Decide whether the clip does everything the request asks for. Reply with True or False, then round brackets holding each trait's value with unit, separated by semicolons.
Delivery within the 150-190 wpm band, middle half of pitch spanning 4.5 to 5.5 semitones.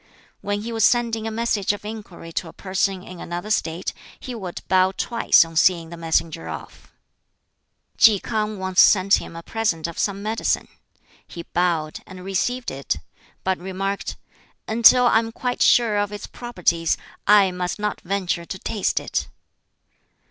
False (165 wpm; 3.8 semitones)